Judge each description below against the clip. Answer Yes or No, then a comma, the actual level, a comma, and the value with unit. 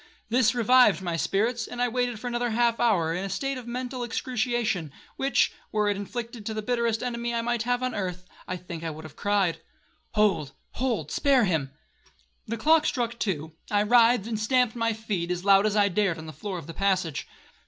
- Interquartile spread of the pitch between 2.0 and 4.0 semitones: No, average, 4.6 semitones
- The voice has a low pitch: No, high, 220 Hz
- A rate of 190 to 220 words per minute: Yes, average, 200 wpm